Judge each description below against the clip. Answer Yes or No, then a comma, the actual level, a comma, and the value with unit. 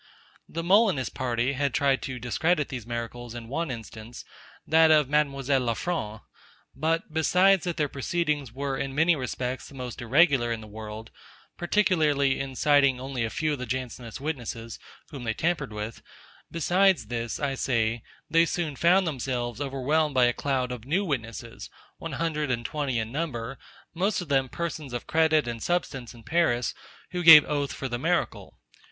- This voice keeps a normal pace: Yes, average, 170 wpm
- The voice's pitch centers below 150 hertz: Yes, low, 135 Hz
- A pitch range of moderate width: Yes, average, 4.8 semitones